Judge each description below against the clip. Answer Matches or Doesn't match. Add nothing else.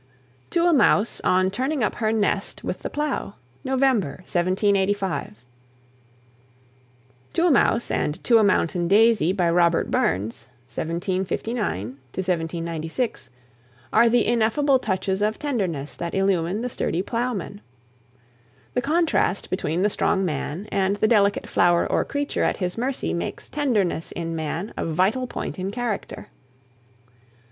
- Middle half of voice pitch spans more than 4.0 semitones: Matches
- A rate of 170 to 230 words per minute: Doesn't match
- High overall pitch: Matches